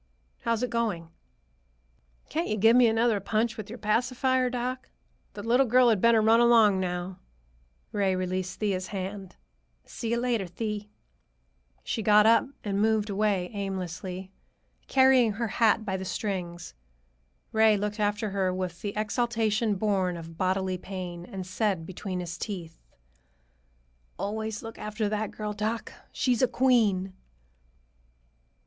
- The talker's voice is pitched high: Yes, high, 210 Hz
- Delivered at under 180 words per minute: Yes, average, 140 wpm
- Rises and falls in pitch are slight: No, average, 3.3 semitones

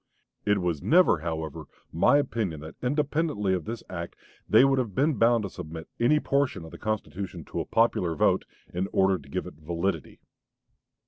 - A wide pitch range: Yes, wide, 6.8 semitones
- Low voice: Yes, low, 100 Hz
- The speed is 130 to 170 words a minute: No, average, 180 wpm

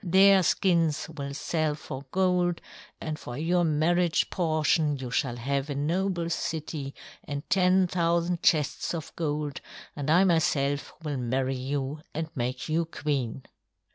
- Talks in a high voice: No, medium, 155 Hz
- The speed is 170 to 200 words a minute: No, average, 140 wpm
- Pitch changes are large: No, average, 3.5 semitones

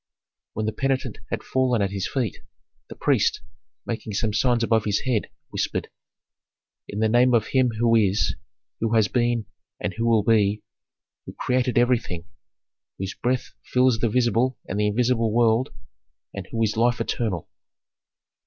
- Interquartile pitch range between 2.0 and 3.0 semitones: Yes, narrow, 2.4 semitones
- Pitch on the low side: Yes, low, 115 Hz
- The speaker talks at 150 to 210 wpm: Yes, average, 155 wpm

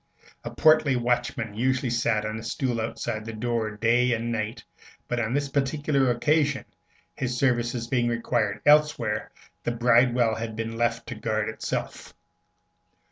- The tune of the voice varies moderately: No, narrow, 2.3 semitones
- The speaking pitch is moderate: No, low, 120 Hz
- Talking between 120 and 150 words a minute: Yes, average, 145 wpm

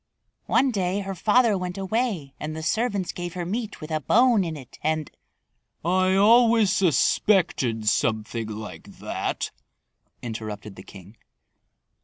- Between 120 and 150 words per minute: Yes, average, 140 wpm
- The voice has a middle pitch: Yes, medium, 180 Hz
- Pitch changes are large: Yes, wide, 8.7 semitones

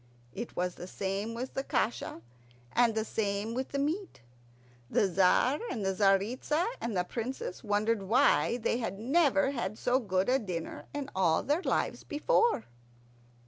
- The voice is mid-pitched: No, high, 225 Hz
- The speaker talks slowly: No, average, 160 wpm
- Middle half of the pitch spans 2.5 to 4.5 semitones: No, average, 5.3 semitones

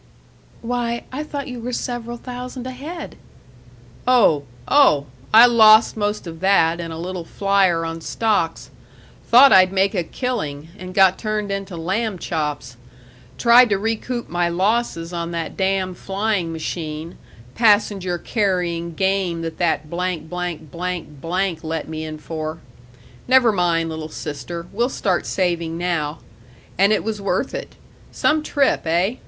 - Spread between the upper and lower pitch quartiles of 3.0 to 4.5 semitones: No, average, 5.1 semitones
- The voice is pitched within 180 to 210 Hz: Yes, medium, 185 Hz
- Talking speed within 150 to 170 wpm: No, slow, 135 wpm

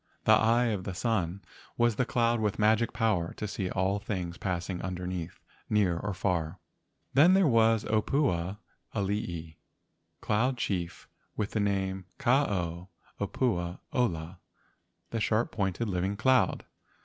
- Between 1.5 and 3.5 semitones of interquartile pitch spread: No, average, 4.1 semitones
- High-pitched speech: No, low, 100 Hz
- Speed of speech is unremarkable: Yes, average, 145 wpm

